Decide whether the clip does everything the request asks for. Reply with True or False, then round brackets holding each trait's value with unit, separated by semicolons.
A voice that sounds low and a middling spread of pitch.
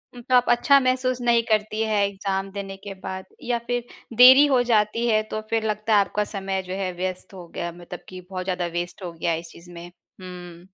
False (200 Hz; 4.1 semitones)